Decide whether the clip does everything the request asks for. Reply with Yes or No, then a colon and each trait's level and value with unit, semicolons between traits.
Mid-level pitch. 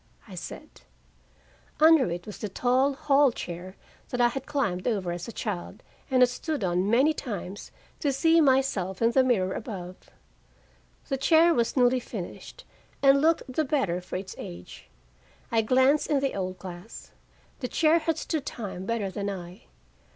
No: high, 240 Hz